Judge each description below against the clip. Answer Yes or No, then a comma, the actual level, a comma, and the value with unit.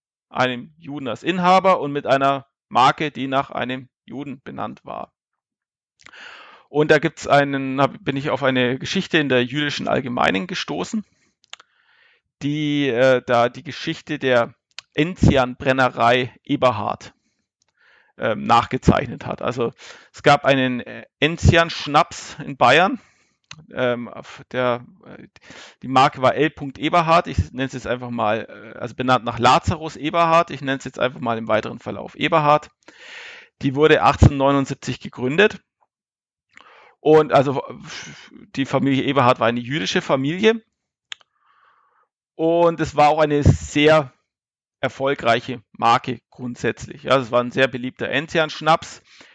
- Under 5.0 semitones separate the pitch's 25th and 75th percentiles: Yes, average, 3.6 semitones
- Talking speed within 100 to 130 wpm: Yes, slow, 125 wpm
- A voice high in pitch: No, low, 135 Hz